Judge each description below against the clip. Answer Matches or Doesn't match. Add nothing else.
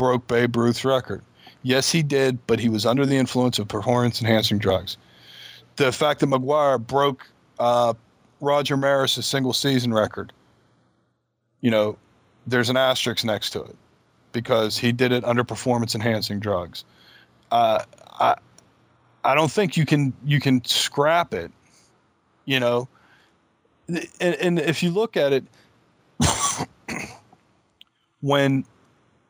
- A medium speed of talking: Doesn't match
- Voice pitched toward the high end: Doesn't match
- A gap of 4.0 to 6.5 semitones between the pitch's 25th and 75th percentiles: Doesn't match